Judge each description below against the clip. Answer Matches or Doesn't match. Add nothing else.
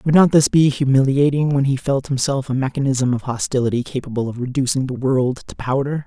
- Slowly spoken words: Doesn't match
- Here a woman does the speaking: Doesn't match